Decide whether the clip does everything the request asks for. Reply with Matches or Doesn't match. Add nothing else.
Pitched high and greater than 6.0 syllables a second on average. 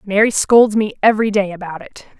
Doesn't match